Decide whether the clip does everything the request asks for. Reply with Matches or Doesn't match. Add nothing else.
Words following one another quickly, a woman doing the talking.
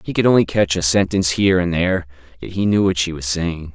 Doesn't match